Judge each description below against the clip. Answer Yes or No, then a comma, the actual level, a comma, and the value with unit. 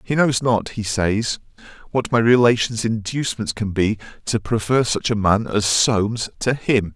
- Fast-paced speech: No, average, 175 wpm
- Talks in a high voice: No, low, 110 Hz